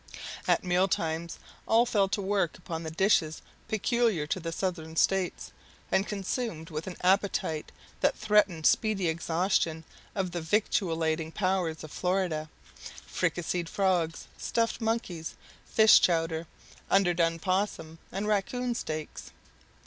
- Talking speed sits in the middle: No, slow, 125 wpm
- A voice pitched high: No, medium, 180 Hz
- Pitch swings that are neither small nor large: Yes, average, 3.6 semitones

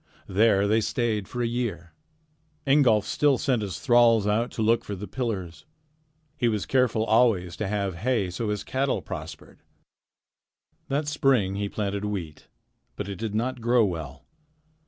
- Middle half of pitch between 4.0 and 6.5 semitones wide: No, average, 3.5 semitones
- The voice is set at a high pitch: No, low, 110 Hz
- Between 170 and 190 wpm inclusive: No, average, 155 wpm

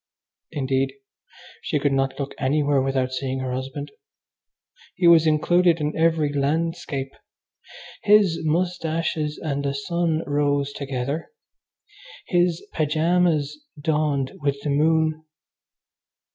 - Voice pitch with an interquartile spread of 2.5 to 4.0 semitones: Yes, average, 2.8 semitones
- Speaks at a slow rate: Yes, slow, 105 wpm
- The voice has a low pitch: No, medium, 150 Hz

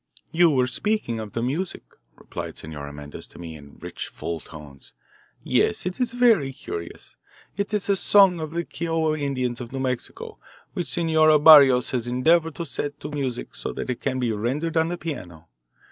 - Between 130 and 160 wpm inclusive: No, average, 185 wpm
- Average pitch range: No, wide, 6.0 semitones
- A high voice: No, medium, 140 Hz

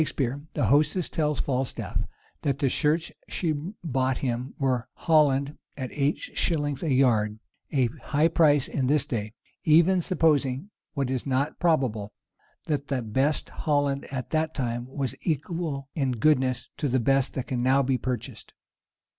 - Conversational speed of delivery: Yes, average, 155 wpm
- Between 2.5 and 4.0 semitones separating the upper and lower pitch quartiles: Yes, average, 2.9 semitones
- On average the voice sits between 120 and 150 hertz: Yes, medium, 140 Hz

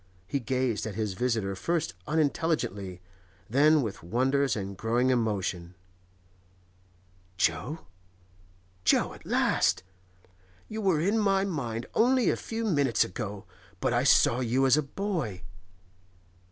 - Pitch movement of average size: No, wide, 8.1 semitones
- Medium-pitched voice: No, low, 120 Hz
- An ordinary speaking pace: No, slow, 120 wpm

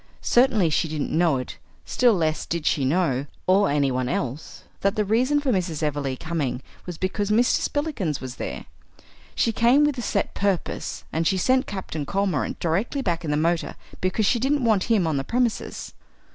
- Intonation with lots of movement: Yes, wide, 6.8 semitones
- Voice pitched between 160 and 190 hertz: Yes, medium, 185 Hz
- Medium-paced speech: Yes, average, 185 wpm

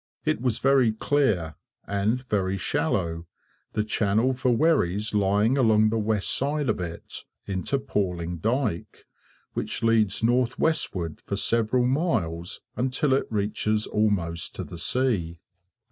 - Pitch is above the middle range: No, low, 110 Hz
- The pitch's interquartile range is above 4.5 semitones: Yes, average, 5.2 semitones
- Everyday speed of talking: No, slow, 130 wpm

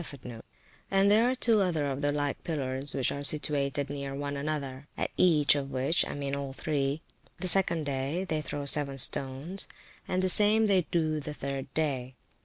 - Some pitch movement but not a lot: Yes, average, 3.5 semitones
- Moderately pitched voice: Yes, medium, 145 Hz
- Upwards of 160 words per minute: Yes, average, 195 wpm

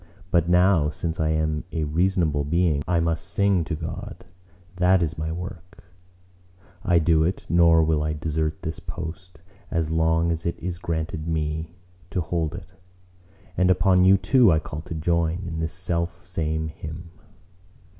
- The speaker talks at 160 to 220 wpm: Yes, average, 165 wpm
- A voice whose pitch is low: Yes, very low, 85 Hz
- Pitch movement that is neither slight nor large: No, narrow, 2.0 semitones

